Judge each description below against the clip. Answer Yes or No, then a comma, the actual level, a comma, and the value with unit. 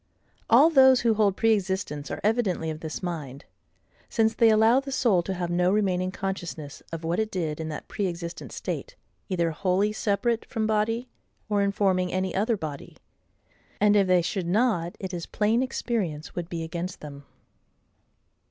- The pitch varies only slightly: No, average, 4.3 semitones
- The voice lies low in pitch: No, high, 190 Hz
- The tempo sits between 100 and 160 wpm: No, average, 170 wpm